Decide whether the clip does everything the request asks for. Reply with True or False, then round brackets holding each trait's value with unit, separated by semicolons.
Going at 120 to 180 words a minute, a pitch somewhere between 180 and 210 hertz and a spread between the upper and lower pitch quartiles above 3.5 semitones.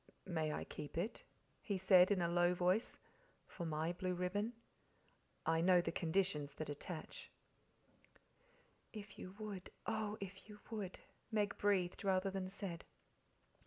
False (140 wpm; 185 Hz; 2.7 semitones)